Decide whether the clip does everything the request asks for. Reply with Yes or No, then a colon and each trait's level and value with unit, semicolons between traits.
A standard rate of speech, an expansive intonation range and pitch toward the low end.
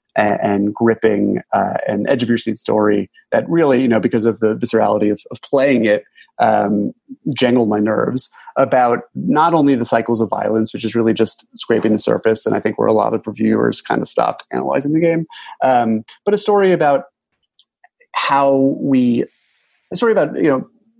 Yes: average, 185 wpm; wide, 7.0 semitones; low, 120 Hz